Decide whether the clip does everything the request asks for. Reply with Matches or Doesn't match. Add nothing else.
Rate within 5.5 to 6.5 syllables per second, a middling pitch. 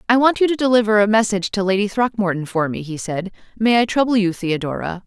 Doesn't match